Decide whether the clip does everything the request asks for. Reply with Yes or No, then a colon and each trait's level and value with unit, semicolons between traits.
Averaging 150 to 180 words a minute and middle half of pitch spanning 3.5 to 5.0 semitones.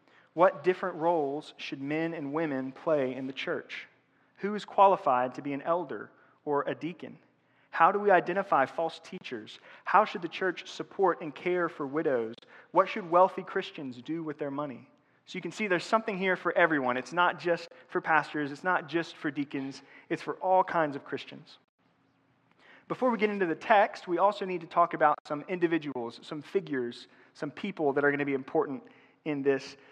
No: average, 190 wpm; average, 4.2 semitones